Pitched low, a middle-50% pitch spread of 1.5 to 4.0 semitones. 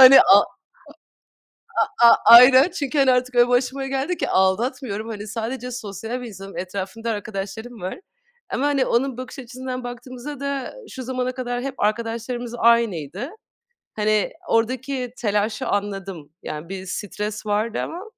No: high, 235 Hz; average, 3.7 semitones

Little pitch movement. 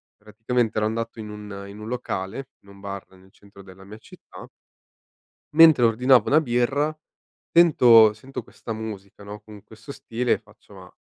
No: average, 3.5 semitones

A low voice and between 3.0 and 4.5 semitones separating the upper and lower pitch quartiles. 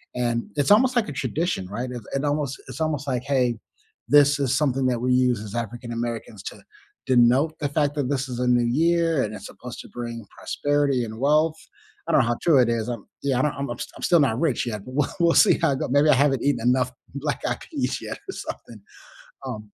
Yes: low, 130 Hz; average, 3.4 semitones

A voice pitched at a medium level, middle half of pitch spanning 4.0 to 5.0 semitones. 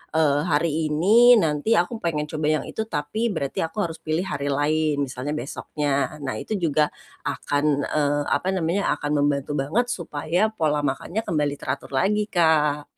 No: medium, 150 Hz; average, 2.9 semitones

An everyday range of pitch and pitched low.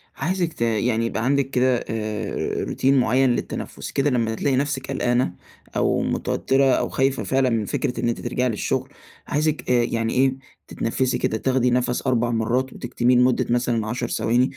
No: narrow, 2.2 semitones; low, 125 Hz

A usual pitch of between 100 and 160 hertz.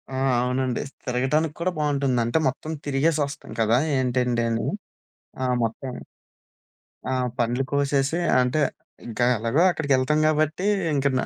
Yes: low, 135 Hz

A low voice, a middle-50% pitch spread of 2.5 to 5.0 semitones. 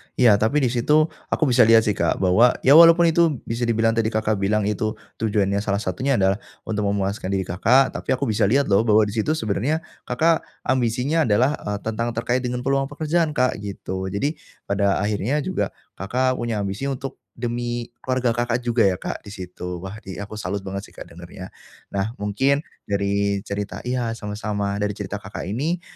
Yes: low, 110 Hz; average, 4.1 semitones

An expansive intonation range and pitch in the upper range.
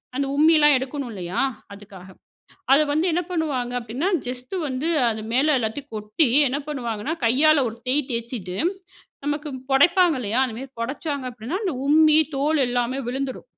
No: average, 4.2 semitones; very high, 265 Hz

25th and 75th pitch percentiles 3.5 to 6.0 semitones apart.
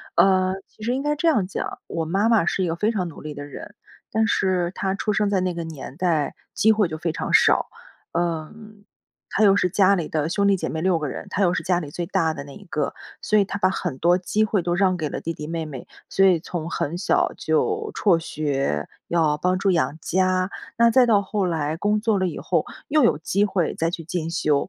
Yes: average, 3.8 semitones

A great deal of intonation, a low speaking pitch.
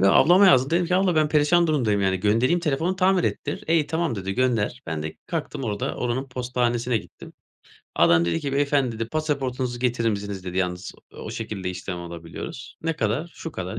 Yes: wide, 7.4 semitones; low, 125 Hz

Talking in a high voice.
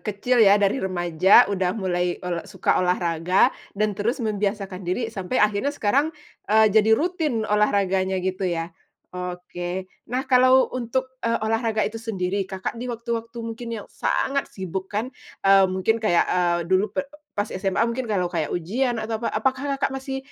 Yes: high, 205 Hz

